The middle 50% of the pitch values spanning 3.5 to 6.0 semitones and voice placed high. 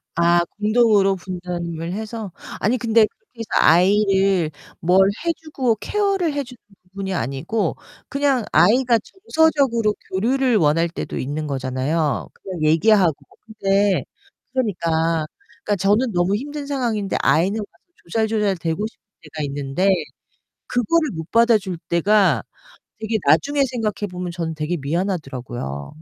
Yes: wide, 5.6 semitones; high, 195 Hz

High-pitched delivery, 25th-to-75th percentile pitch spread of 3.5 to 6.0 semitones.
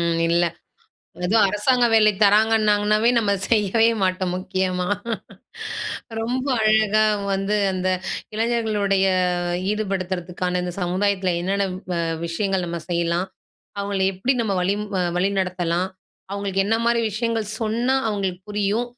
No: high, 200 Hz; average, 2.8 semitones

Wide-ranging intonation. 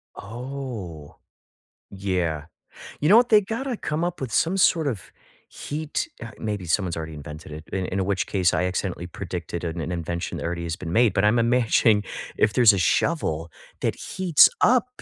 Yes: wide, 8.6 semitones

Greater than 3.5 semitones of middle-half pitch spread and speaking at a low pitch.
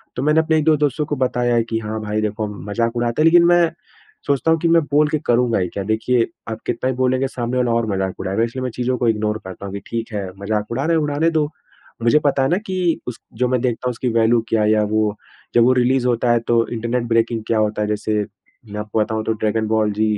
No: average, 3.2 semitones; low, 120 Hz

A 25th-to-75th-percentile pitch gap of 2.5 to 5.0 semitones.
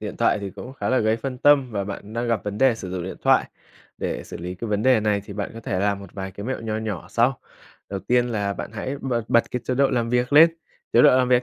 Yes: average, 3.9 semitones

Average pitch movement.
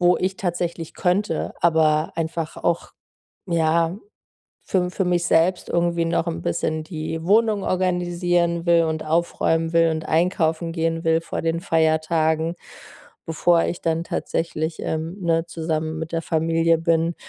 No: narrow, 1.3 semitones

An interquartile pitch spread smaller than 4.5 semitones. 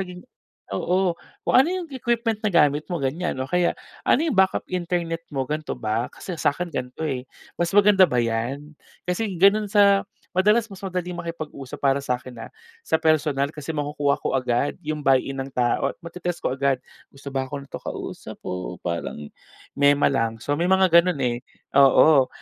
No: average, 5.2 semitones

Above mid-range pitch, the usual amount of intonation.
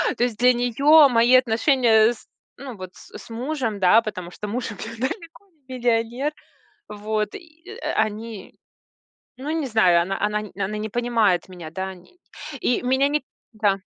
Yes: high, 230 Hz; average, 3.7 semitones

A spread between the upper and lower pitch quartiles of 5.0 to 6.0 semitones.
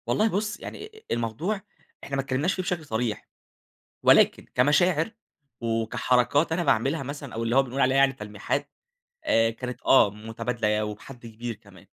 Yes: average, 5.3 semitones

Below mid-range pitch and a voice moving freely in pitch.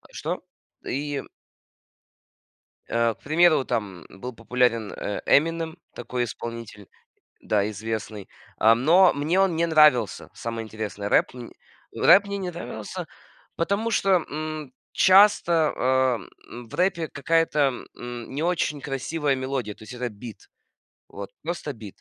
Yes: low, 130 Hz; wide, 6.2 semitones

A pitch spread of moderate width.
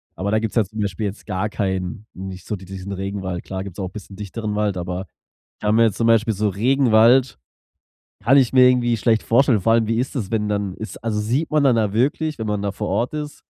Yes: average, 3.1 semitones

